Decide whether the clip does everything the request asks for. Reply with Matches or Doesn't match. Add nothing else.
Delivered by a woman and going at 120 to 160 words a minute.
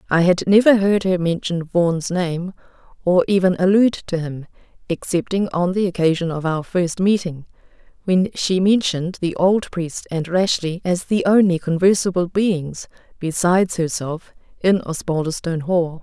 Matches